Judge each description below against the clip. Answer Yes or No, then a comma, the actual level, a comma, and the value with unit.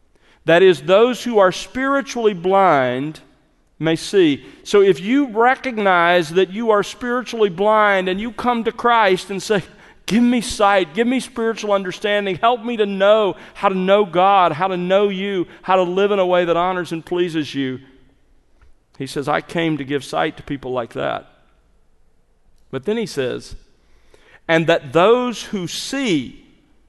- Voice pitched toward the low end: No, high, 195 Hz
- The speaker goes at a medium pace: Yes, average, 165 wpm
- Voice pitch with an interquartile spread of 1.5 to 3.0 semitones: No, wide, 5.4 semitones